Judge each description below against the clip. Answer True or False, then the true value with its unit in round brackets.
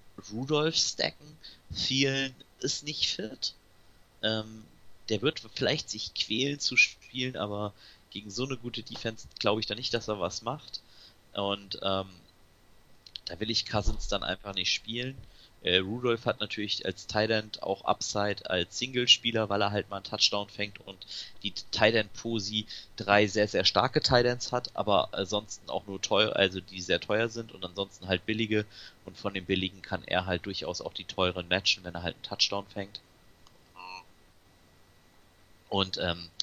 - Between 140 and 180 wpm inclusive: True (160 wpm)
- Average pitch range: True (3.2 semitones)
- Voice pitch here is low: True (100 Hz)